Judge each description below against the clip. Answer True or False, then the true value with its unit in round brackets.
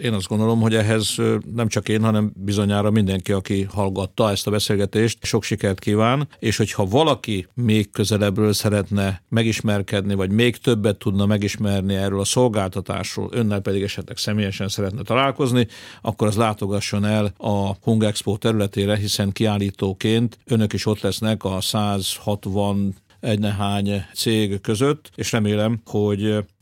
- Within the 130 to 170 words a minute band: True (140 wpm)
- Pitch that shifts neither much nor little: False (1.9 semitones)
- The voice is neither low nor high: False (105 Hz)